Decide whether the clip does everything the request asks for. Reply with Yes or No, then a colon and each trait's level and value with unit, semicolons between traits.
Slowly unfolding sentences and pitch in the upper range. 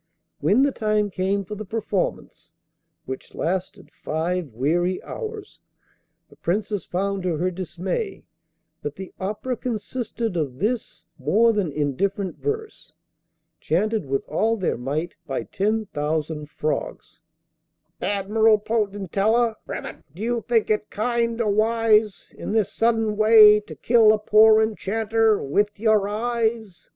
Yes: slow, 130 wpm; high, 210 Hz